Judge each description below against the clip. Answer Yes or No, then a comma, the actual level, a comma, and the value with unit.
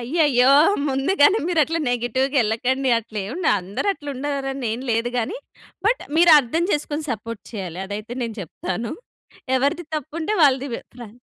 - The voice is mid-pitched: No, very high, 260 Hz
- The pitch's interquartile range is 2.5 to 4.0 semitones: No, average, 4.5 semitones